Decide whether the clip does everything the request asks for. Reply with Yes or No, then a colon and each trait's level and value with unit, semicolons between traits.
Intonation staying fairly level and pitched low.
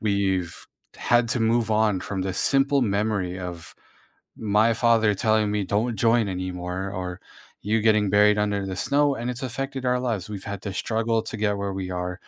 No: average, 3.1 semitones; low, 105 Hz